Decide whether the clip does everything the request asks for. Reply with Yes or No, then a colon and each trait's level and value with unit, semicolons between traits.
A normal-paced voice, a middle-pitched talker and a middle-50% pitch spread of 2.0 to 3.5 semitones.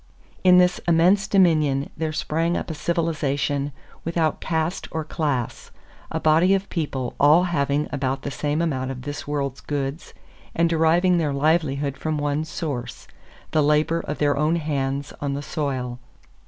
Yes: average, 155 wpm; medium, 150 Hz; average, 2.9 semitones